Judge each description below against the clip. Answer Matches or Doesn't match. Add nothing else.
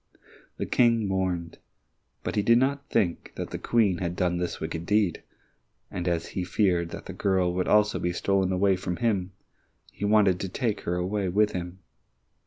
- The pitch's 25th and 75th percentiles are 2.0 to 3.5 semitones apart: Matches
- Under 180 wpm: Doesn't match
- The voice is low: Matches